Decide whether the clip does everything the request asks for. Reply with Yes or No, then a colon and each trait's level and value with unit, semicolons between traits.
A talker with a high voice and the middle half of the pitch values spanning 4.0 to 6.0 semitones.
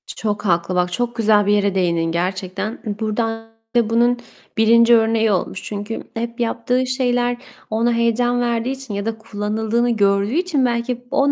No: high, 225 Hz; narrow, 2.6 semitones